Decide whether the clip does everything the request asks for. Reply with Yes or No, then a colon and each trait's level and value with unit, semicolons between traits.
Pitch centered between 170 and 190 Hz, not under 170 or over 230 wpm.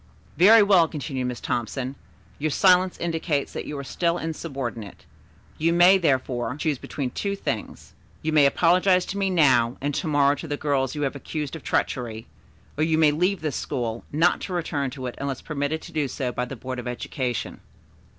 No: medium, 145 Hz; average, 190 wpm